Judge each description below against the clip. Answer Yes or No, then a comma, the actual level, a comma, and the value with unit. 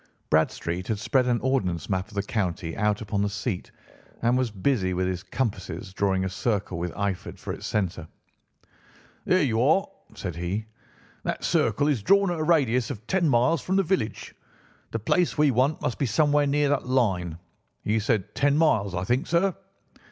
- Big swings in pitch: Yes, wide, 7.0 semitones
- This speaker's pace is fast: No, average, 185 wpm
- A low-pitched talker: Yes, low, 110 Hz